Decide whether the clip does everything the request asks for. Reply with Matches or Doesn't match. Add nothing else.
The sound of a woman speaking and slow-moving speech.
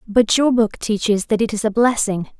Doesn't match